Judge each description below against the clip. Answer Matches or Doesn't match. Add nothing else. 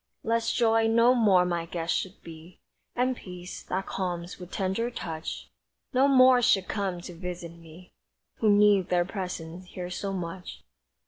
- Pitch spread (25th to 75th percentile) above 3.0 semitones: Matches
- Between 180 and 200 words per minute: Doesn't match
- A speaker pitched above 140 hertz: Matches